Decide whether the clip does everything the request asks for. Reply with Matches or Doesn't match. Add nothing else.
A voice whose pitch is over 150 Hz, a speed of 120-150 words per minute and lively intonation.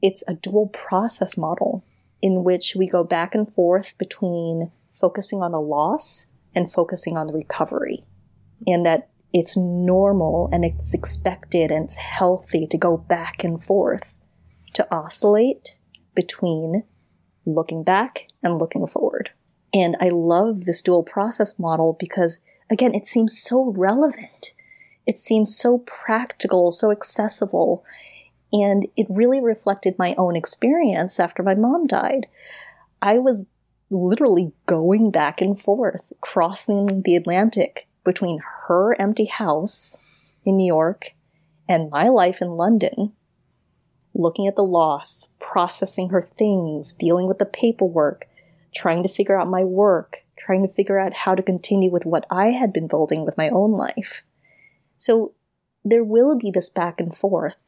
Doesn't match